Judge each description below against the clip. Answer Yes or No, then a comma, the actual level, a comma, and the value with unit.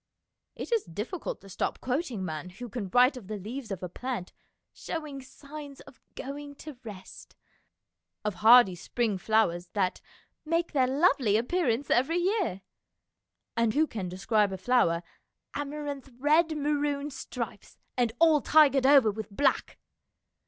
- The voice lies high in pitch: Yes, very high, 250 Hz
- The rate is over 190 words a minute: No, average, 155 wpm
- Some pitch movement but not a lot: No, wide, 5.7 semitones